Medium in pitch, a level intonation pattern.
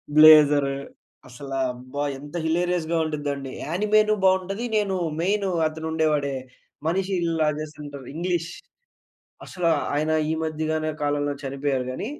No: medium, 155 Hz; average, 3.6 semitones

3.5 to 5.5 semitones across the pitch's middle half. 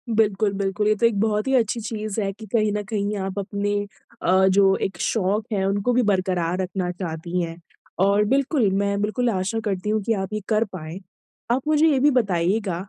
No: narrow, 2.5 semitones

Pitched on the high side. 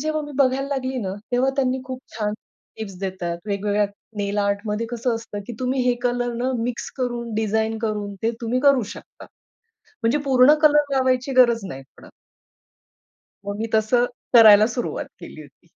Yes: high, 235 Hz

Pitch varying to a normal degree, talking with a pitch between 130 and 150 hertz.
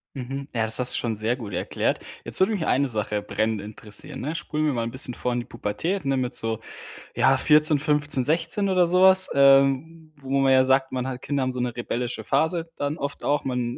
Yes: average, 3.9 semitones; low, 135 Hz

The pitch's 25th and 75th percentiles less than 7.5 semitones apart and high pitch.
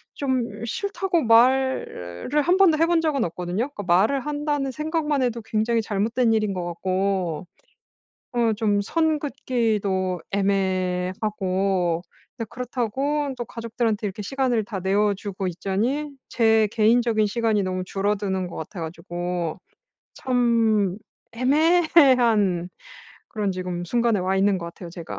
Yes: average, 5.3 semitones; high, 215 Hz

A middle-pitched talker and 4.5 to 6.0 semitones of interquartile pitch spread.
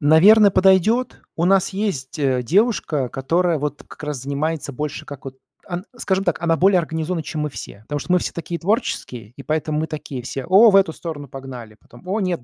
Yes: medium, 160 Hz; average, 5.0 semitones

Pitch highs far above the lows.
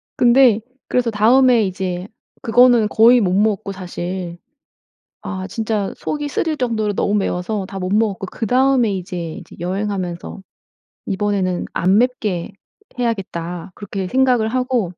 No: average, 4.3 semitones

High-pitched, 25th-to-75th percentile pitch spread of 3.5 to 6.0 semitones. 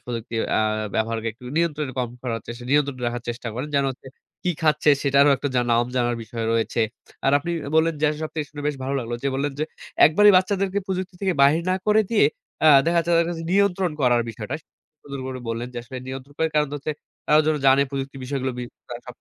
No: medium, 140 Hz; average, 4.6 semitones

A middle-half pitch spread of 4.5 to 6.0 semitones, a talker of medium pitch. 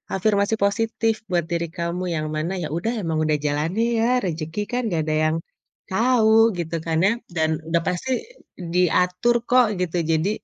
Yes: average, 5.3 semitones; medium, 180 Hz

